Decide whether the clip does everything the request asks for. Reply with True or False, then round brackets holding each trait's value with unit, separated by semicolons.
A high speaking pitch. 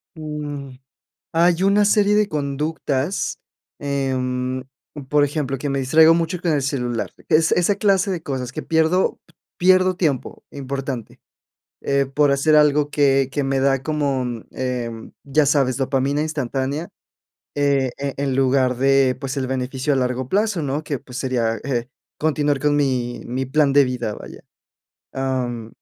False (140 Hz)